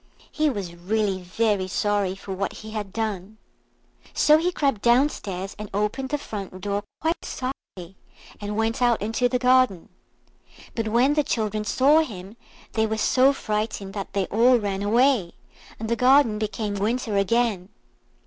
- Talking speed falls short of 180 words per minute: Yes, average, 160 wpm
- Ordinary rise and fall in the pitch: Yes, average, 4.0 semitones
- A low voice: No, high, 215 Hz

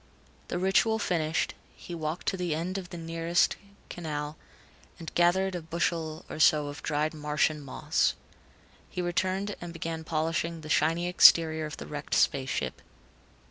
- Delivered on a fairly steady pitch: Yes, narrow, 2.2 semitones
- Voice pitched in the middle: Yes, medium, 165 Hz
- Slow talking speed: No, average, 155 wpm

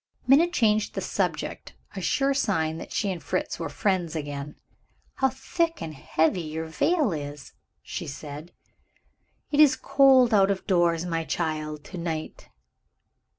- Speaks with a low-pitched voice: No, medium, 175 Hz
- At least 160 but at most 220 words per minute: No, average, 150 wpm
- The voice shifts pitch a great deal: Yes, wide, 8.5 semitones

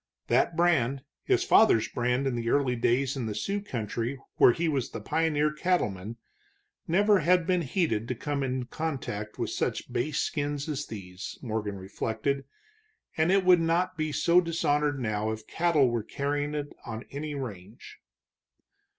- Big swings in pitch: Yes, wide, 5.8 semitones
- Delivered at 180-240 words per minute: No, average, 160 wpm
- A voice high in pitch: No, medium, 140 Hz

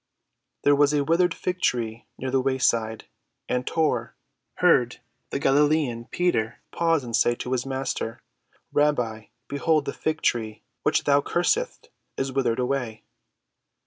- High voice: No, low, 135 Hz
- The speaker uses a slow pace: Yes, slow, 130 wpm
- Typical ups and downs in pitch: Yes, average, 4.0 semitones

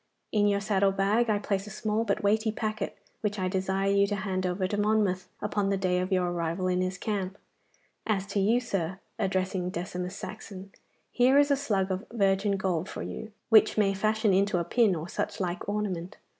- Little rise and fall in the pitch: Yes, narrow, 2.2 semitones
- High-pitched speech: Yes, high, 195 Hz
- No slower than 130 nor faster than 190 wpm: No, average, 200 wpm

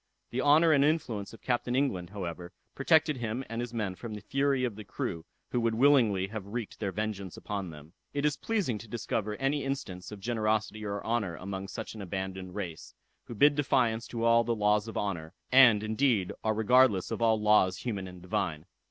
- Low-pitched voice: Yes, low, 110 Hz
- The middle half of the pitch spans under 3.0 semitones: No, average, 4.2 semitones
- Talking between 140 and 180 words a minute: No, average, 200 wpm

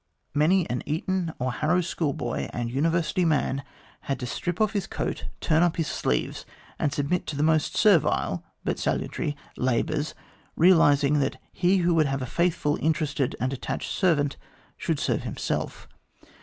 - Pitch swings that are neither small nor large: Yes, average, 3.7 semitones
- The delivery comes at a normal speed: Yes, average, 155 wpm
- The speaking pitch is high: No, medium, 155 Hz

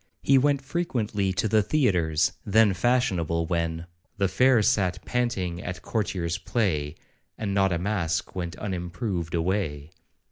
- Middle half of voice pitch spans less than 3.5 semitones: No, average, 4.5 semitones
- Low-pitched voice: Yes, very low, 95 Hz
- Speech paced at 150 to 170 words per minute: No, average, 140 wpm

